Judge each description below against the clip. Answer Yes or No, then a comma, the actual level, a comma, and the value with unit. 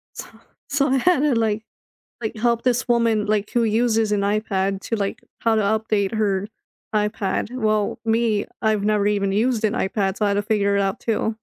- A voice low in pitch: No, high, 215 Hz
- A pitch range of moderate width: No, narrow, 2.0 semitones